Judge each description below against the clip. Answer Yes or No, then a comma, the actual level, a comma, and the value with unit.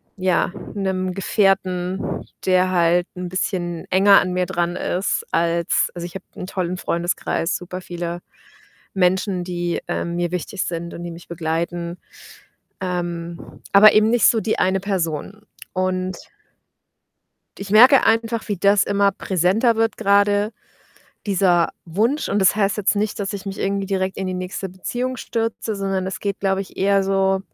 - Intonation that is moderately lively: No, narrow, 2.3 semitones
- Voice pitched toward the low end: No, high, 190 Hz